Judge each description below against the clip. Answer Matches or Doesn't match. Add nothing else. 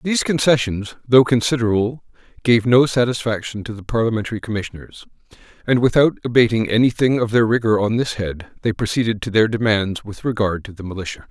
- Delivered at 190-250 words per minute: Doesn't match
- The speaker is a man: Matches